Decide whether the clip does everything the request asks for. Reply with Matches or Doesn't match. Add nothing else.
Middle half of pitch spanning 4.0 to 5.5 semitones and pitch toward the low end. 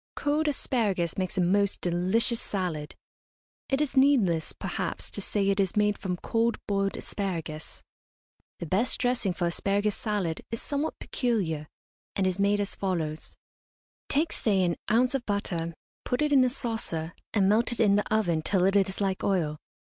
Doesn't match